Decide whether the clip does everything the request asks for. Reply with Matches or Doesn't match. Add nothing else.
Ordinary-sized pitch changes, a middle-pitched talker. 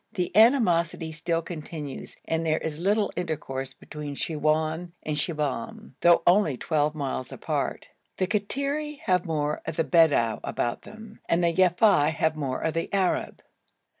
Matches